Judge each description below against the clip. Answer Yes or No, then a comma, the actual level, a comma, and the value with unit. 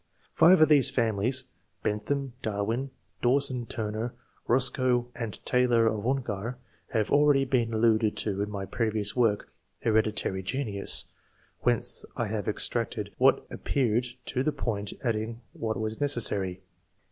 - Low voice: Yes, low, 115 Hz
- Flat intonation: No, average, 3.2 semitones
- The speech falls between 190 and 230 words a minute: No, average, 140 wpm